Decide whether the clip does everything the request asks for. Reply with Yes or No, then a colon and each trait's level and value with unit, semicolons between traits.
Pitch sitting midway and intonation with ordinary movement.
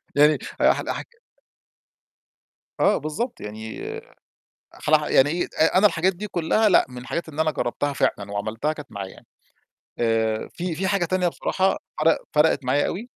No: medium, 155 Hz; wide, 6.5 semitones